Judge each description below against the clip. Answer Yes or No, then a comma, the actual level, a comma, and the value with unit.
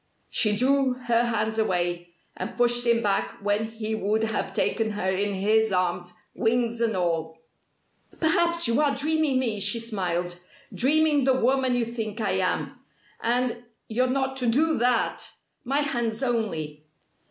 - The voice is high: Yes, high, 230 Hz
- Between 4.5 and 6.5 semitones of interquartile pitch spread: No, average, 3.8 semitones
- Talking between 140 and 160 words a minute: Yes, average, 155 wpm